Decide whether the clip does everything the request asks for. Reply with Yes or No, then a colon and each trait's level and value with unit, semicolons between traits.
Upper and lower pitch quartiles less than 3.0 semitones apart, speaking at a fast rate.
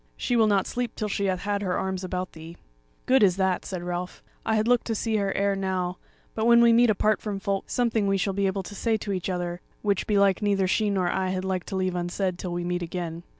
Yes: narrow, 2.5 semitones; fast, 255 wpm